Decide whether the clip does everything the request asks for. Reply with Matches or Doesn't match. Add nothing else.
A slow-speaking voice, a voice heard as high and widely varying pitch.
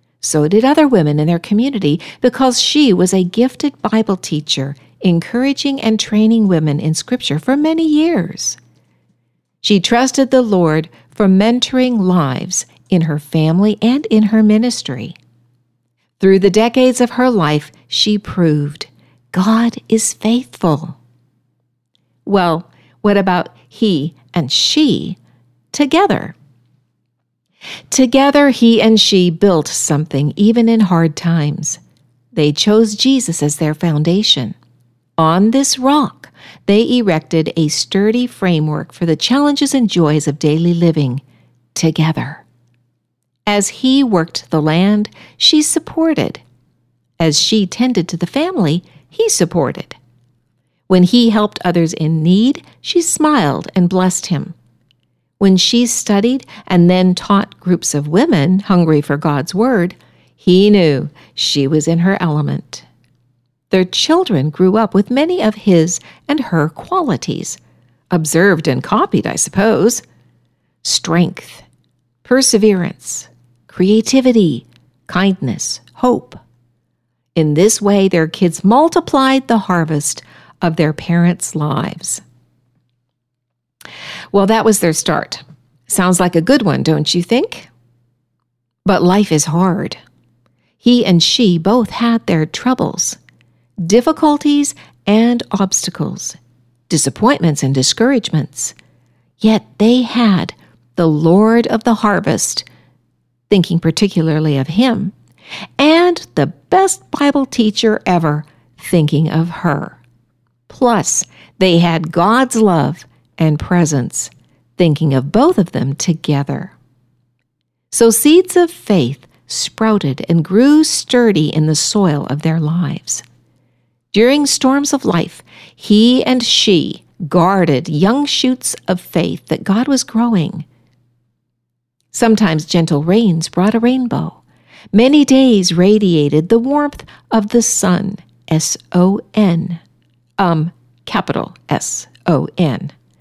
Doesn't match